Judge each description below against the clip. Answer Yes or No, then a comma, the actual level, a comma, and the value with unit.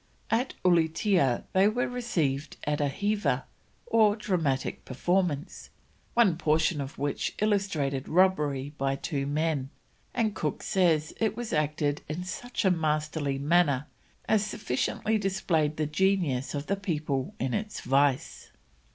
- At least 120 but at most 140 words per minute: Yes, slow, 135 wpm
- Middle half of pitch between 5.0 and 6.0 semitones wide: Yes, wide, 5.5 semitones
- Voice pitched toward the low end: No, medium, 160 Hz